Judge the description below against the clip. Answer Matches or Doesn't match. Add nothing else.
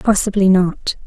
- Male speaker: Doesn't match